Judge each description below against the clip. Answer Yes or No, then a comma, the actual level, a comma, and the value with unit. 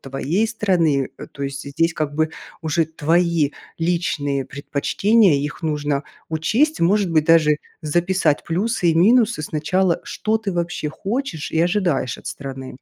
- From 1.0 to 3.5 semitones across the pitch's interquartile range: No, average, 4.3 semitones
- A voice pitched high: No, medium, 165 Hz